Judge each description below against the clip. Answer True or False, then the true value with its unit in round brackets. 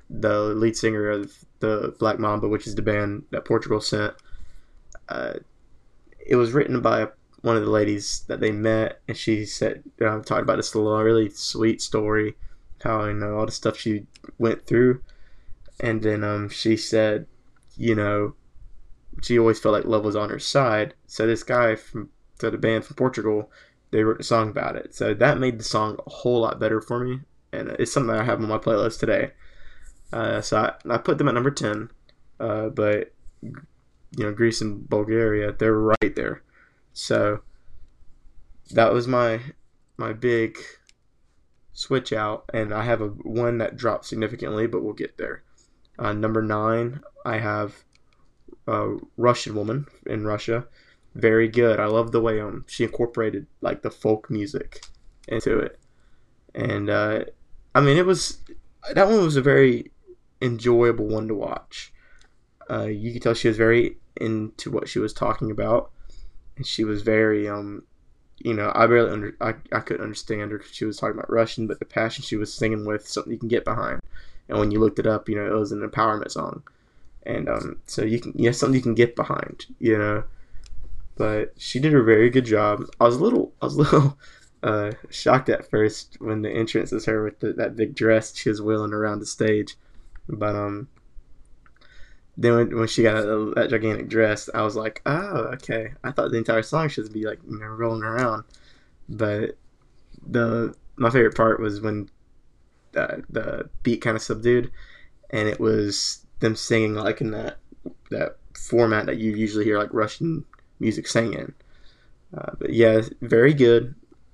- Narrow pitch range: True (1.8 semitones)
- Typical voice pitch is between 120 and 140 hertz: False (110 Hz)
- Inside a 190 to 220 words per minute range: False (180 wpm)